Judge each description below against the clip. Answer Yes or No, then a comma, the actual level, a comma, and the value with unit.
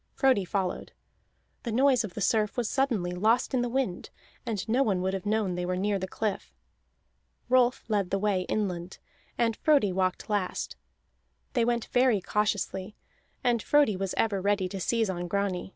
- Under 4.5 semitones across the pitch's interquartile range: Yes, average, 3.9 semitones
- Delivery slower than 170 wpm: No, average, 175 wpm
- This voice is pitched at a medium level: No, high, 205 Hz